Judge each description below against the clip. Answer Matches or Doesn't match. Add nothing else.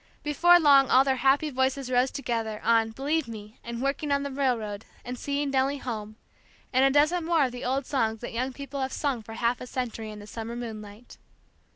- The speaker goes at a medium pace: Doesn't match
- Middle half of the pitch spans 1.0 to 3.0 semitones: Doesn't match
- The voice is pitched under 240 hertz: Doesn't match